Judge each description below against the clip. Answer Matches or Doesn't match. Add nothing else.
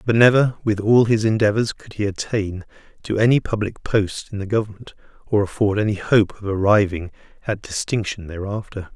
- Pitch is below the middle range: Matches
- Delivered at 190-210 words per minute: Doesn't match